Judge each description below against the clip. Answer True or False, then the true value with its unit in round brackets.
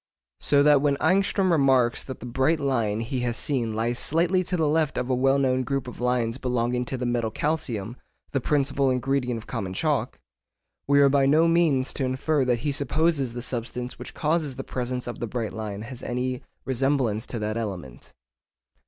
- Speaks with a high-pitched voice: False (130 Hz)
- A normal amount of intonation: True (3.0 semitones)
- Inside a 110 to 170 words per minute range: False (195 wpm)